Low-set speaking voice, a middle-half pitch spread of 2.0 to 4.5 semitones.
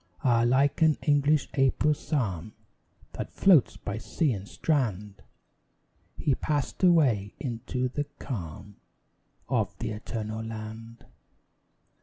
No: low, 120 Hz; average, 5.1 semitones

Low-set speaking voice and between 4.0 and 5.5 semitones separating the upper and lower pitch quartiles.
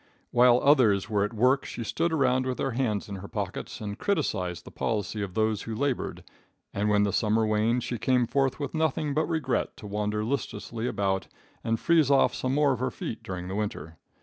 Yes: low, 115 Hz; average, 4.5 semitones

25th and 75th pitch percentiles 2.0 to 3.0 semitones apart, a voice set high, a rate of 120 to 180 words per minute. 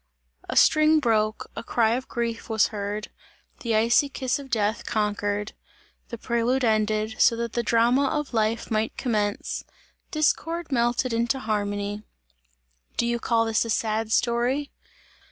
Yes: narrow, 2.4 semitones; high, 230 Hz; average, 145 wpm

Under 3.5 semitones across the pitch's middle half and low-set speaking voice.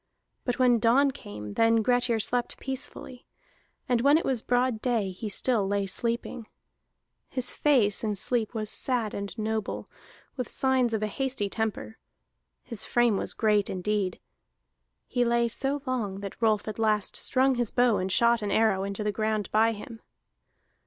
No: average, 2.9 semitones; high, 225 Hz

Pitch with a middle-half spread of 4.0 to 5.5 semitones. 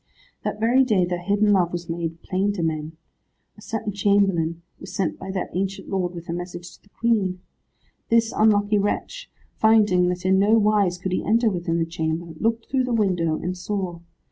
No: average, 3.2 semitones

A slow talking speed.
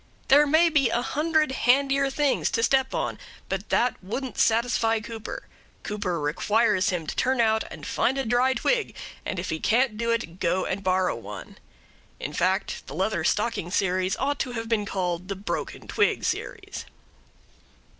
No: average, 170 wpm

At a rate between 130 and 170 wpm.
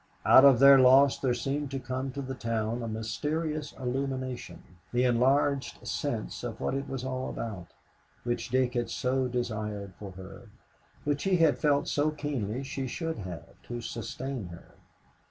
Yes: average, 165 wpm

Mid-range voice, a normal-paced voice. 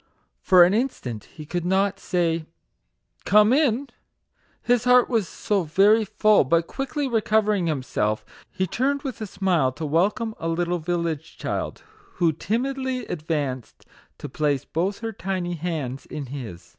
Yes: medium, 180 Hz; average, 155 wpm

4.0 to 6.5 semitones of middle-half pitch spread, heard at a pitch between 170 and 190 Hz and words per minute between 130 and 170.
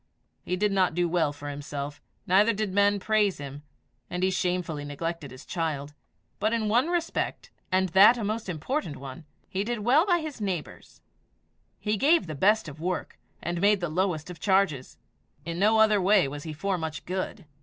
No: average, 5.0 semitones; medium, 185 Hz; average, 185 wpm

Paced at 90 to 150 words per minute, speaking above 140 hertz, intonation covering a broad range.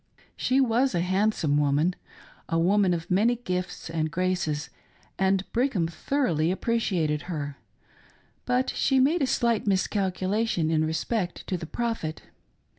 Yes: slow, 135 wpm; medium, 185 Hz; wide, 5.9 semitones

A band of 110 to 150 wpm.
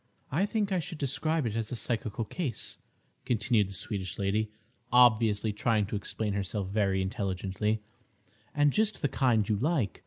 No: average, 160 wpm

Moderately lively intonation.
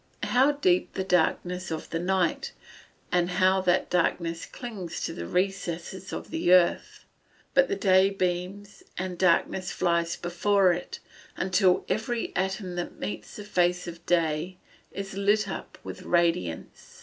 No: narrow, 1.9 semitones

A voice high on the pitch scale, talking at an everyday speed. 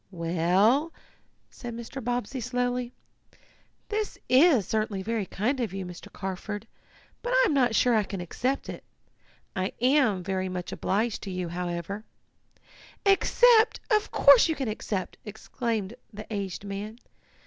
Yes: high, 220 Hz; average, 145 wpm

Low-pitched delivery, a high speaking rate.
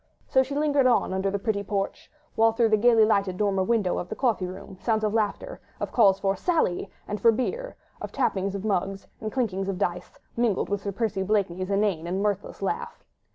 No: high, 205 Hz; fast, 210 wpm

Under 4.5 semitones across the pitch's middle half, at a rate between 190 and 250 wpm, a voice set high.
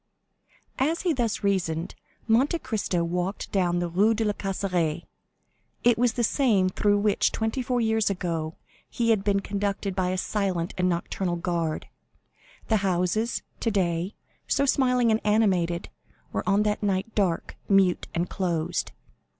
No: average, 3.9 semitones; average, 150 wpm; high, 195 Hz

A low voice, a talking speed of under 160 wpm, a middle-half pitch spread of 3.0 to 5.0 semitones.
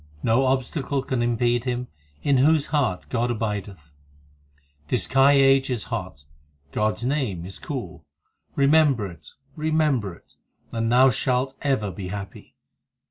Yes: low, 125 Hz; slow, 135 wpm; average, 4.5 semitones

